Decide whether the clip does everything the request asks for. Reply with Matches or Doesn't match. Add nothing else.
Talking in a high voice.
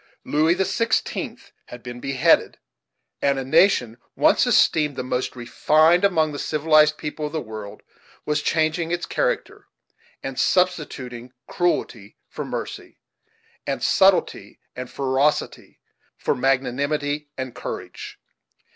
Doesn't match